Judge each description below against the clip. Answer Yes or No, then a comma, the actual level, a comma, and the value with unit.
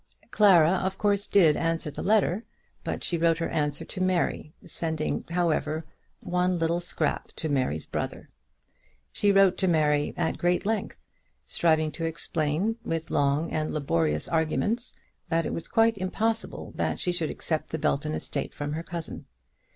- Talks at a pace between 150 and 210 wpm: Yes, average, 160 wpm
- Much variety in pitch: No, average, 3.2 semitones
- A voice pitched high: No, medium, 165 Hz